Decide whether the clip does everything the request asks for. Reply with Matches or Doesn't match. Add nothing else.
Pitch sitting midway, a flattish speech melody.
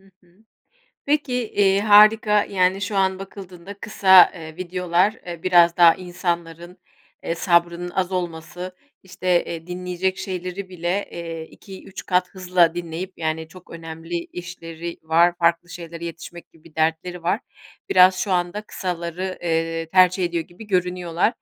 Matches